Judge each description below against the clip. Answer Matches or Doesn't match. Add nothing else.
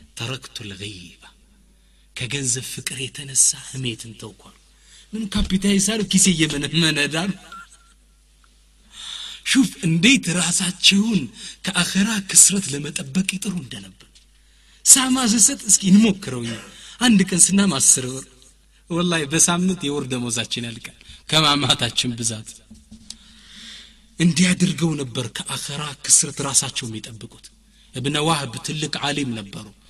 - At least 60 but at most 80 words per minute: Doesn't match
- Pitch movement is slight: Doesn't match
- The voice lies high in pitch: Doesn't match